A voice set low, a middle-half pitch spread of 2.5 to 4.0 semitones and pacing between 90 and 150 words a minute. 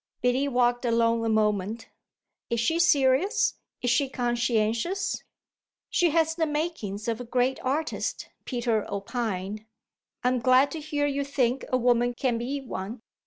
No: high, 245 Hz; average, 3.5 semitones; average, 145 wpm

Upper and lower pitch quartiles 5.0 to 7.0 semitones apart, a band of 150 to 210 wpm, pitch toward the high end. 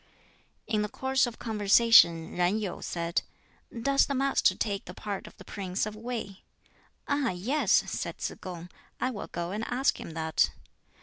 Yes: wide, 5.4 semitones; average, 170 wpm; high, 210 Hz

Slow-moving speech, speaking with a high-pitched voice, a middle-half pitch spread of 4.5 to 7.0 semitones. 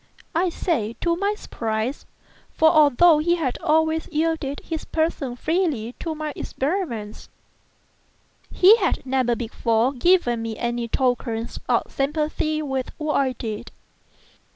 Yes: slow, 130 wpm; very high, 290 Hz; average, 5.2 semitones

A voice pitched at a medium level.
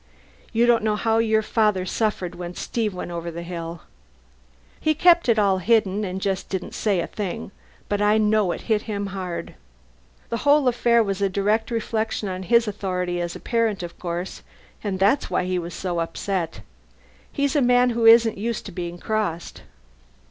No: high, 205 Hz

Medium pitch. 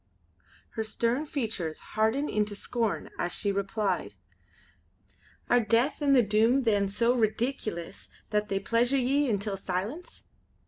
No: high, 220 Hz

